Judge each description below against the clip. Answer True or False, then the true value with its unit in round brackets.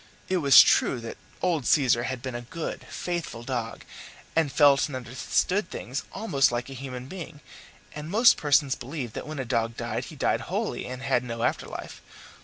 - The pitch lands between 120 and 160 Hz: True (135 Hz)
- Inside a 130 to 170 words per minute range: False (190 wpm)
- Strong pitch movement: False (4.1 semitones)